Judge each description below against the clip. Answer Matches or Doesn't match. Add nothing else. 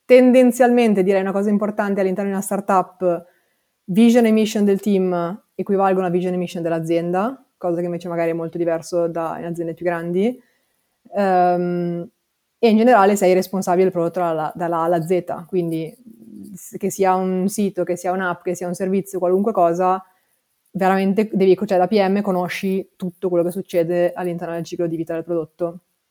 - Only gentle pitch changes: Matches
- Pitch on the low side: Doesn't match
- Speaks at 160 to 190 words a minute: Matches